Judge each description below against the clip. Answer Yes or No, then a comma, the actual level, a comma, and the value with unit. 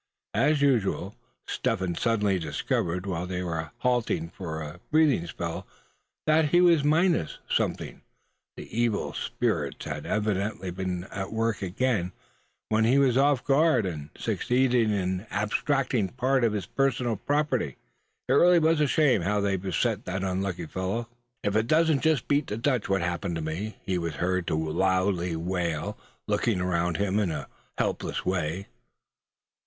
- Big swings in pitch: Yes, wide, 6.4 semitones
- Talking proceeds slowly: No, average, 160 wpm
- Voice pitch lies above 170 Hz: No, low, 100 Hz